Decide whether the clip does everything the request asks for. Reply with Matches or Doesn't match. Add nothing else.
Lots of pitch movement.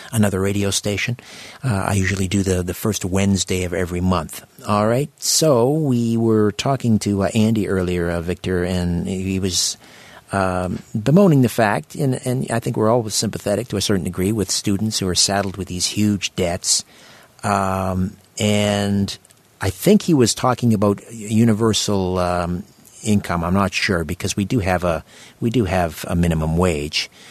Doesn't match